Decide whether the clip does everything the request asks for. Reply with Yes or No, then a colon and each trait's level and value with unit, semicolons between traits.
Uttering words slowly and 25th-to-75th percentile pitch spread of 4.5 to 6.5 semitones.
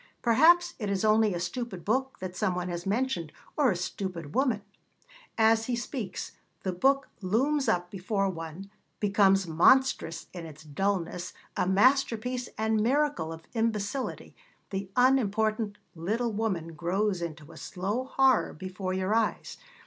No: average, 145 wpm; average, 4.9 semitones